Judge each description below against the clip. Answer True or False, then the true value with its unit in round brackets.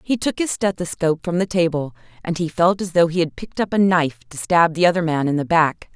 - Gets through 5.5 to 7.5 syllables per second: True (6.1 syllables/s)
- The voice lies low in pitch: False (170 Hz)